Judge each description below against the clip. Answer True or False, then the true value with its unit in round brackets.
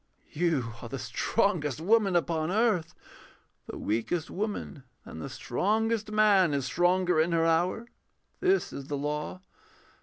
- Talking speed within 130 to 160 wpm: True (145 wpm)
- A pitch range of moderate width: False (5.7 semitones)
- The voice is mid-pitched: True (175 Hz)